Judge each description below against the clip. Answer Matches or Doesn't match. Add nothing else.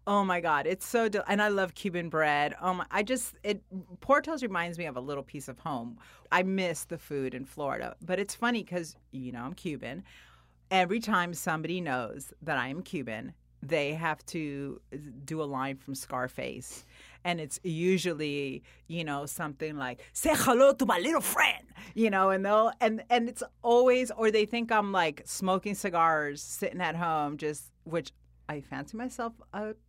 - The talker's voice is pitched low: Doesn't match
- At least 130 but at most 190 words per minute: Matches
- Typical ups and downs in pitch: Doesn't match